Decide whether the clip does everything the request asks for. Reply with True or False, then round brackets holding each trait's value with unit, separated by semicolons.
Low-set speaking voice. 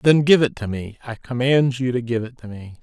True (125 Hz)